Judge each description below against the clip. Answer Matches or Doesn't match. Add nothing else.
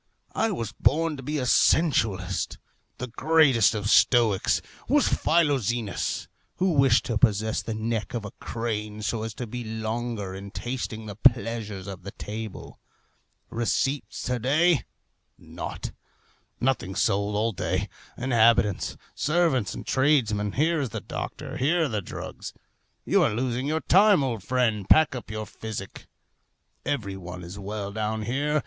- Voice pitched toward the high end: Doesn't match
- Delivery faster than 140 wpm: Matches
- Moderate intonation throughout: Matches